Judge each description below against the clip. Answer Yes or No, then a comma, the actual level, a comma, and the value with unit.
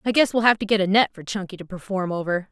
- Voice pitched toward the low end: No, high, 195 Hz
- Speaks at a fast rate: Yes, fast, 310 wpm